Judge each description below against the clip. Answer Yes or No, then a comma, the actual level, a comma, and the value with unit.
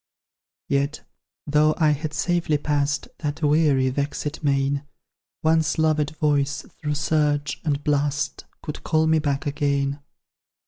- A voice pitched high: No, medium, 150 Hz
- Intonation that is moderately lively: No, narrow, 1.5 semitones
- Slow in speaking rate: Yes, slow, 125 wpm